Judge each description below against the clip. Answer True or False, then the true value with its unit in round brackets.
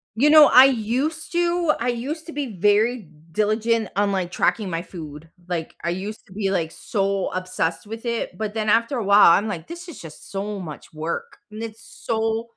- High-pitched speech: True (215 Hz)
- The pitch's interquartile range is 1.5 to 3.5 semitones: False (4.2 semitones)